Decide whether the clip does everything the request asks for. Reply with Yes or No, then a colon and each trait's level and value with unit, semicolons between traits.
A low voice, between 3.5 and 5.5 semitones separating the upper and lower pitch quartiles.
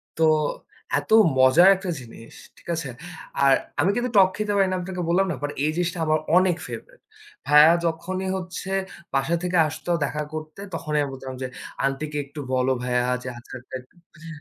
No: medium, 160 Hz; average, 4.9 semitones